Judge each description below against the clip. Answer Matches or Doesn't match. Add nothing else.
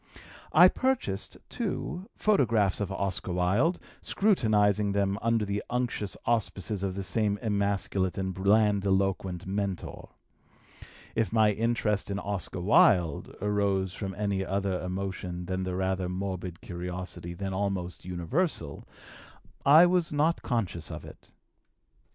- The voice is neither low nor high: Doesn't match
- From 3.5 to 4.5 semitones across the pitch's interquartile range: Doesn't match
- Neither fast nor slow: Doesn't match